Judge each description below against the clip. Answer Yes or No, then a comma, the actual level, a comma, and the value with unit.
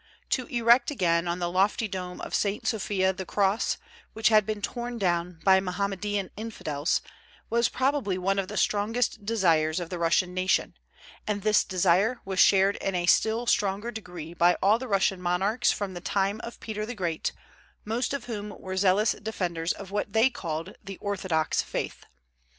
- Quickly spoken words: No, average, 175 wpm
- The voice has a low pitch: No, high, 195 Hz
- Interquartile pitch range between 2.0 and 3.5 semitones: Yes, average, 3.2 semitones